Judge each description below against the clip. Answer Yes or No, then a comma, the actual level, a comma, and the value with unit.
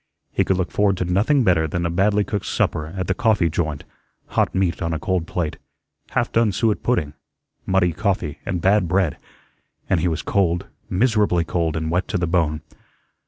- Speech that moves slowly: No, average, 190 wpm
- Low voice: Yes, very low, 90 Hz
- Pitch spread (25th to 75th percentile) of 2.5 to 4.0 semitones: Yes, average, 3.2 semitones